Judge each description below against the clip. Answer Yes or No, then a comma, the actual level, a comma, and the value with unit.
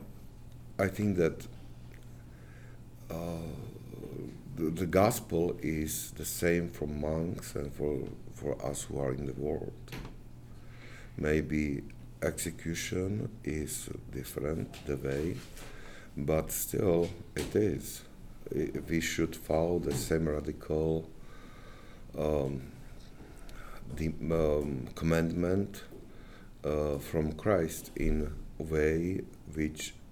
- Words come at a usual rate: No, slow, 95 wpm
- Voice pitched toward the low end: Yes, very low, 75 Hz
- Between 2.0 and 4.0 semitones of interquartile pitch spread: Yes, average, 2.7 semitones